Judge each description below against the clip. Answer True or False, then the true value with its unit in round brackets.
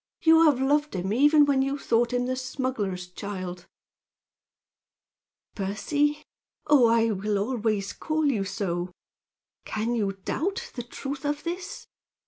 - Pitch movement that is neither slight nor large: False (6.4 semitones)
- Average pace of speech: False (130 wpm)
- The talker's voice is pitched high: True (245 Hz)